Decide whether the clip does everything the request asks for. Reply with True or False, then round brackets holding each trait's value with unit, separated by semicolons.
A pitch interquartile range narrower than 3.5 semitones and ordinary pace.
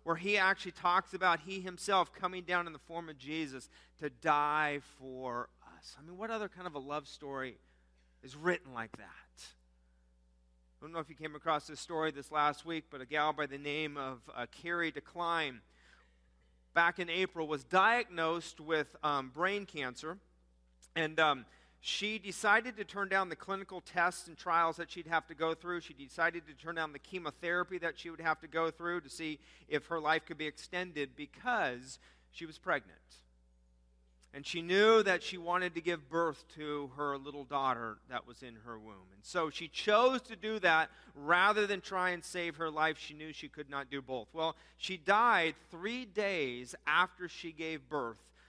False (4.1 semitones; 190 wpm)